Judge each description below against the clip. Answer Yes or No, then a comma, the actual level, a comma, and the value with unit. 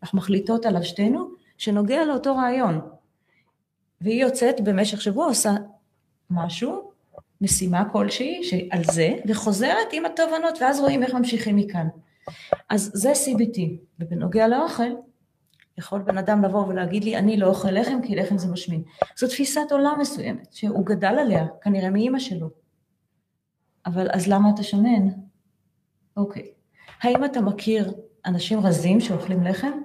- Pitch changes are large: No, average, 4.7 semitones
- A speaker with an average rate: Yes, average, 135 wpm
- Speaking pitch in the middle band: No, high, 205 Hz